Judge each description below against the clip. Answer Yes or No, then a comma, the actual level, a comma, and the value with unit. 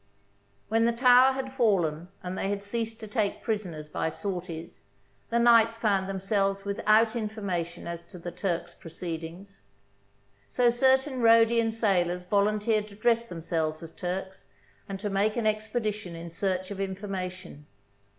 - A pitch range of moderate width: Yes, average, 4.0 semitones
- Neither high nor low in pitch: No, high, 200 Hz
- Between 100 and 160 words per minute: Yes, average, 150 wpm